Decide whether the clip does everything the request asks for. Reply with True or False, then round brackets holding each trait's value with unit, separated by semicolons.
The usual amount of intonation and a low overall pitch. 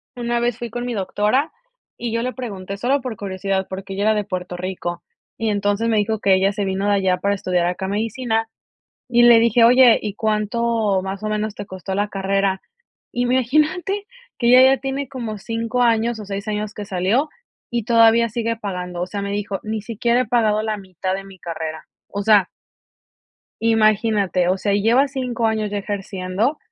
False (3.2 semitones; 215 Hz)